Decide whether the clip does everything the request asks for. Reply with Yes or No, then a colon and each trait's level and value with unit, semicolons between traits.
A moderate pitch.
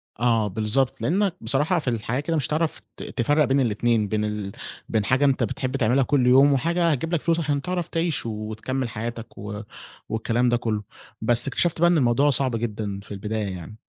No: low, 125 Hz